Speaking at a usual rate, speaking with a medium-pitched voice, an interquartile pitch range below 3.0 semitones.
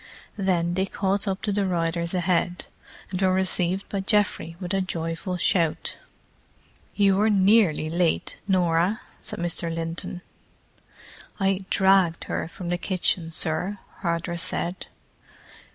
No: slow, 130 wpm; medium, 180 Hz; narrow, 2.4 semitones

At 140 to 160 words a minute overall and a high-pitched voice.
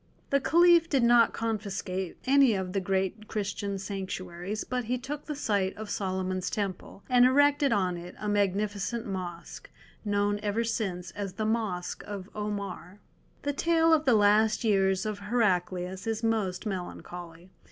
Yes: average, 150 wpm; high, 205 Hz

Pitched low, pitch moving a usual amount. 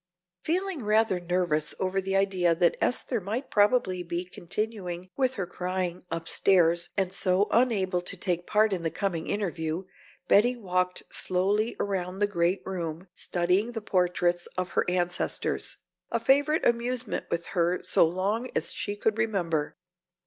No: medium, 185 Hz; average, 3.2 semitones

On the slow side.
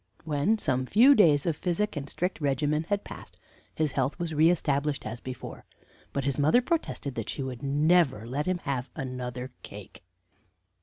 No: average, 170 wpm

